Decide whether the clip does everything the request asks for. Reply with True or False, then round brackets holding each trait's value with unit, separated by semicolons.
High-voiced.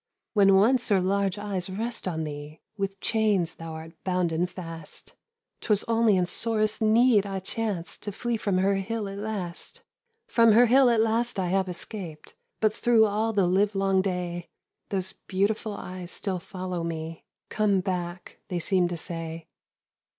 True (195 Hz)